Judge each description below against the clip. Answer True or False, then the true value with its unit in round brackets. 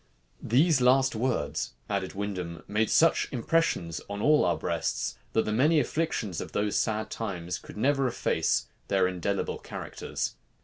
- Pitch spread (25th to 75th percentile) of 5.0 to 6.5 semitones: True (5.6 semitones)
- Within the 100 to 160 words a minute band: True (145 wpm)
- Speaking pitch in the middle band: False (110 Hz)